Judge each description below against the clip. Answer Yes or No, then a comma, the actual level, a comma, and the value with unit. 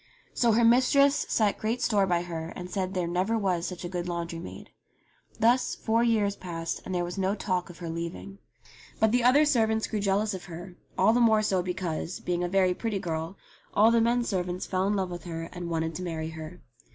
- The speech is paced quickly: Yes, fast, 220 wpm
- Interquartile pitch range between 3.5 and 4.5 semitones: Yes, average, 4.1 semitones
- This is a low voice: No, medium, 185 Hz